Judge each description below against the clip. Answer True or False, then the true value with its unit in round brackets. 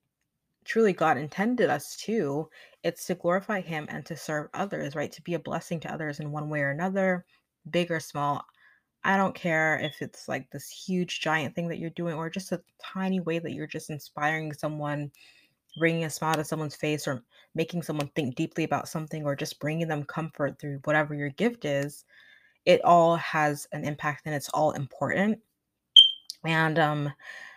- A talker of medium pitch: True (160 Hz)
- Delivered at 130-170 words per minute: False (185 wpm)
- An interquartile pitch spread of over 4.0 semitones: False (2.5 semitones)